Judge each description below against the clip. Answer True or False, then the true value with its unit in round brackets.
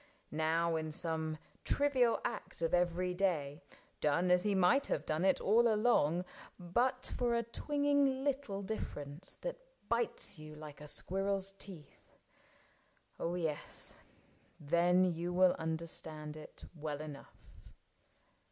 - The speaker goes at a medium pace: False (130 wpm)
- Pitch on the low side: False (180 Hz)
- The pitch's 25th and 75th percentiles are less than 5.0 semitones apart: False (5.3 semitones)